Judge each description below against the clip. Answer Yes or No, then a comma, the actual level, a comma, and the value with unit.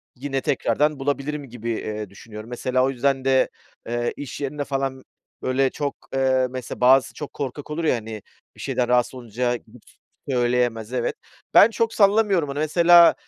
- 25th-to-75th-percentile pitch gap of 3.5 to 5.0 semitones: No, average, 2.9 semitones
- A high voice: No, low, 130 Hz